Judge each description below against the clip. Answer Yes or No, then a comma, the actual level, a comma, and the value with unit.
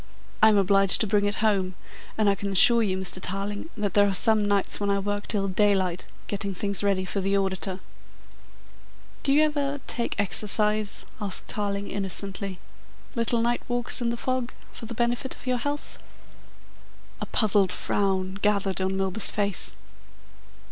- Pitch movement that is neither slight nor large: No, narrow, 2.3 semitones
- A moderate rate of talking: Yes, average, 165 wpm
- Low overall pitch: No, high, 205 Hz